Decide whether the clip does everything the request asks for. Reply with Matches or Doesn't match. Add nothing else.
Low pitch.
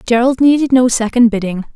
Doesn't match